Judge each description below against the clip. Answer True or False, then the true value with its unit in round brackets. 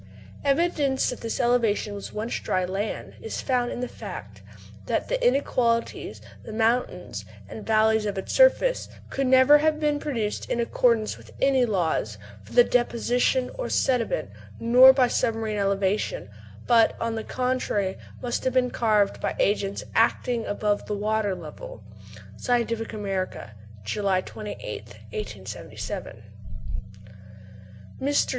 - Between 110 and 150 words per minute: True (135 wpm)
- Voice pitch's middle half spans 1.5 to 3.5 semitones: False (3.9 semitones)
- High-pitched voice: True (225 Hz)